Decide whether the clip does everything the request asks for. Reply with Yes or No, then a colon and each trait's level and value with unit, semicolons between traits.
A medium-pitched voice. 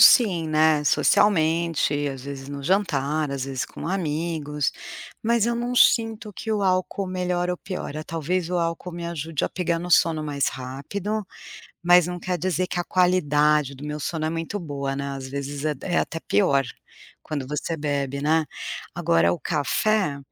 Yes: medium, 160 Hz